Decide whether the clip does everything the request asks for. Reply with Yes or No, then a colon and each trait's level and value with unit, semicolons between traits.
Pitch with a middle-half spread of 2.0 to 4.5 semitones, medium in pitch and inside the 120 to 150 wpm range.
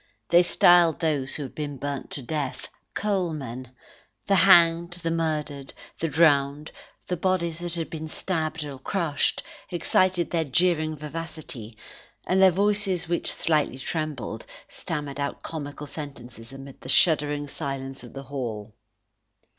Yes: average, 3.6 semitones; medium, 155 Hz; average, 140 wpm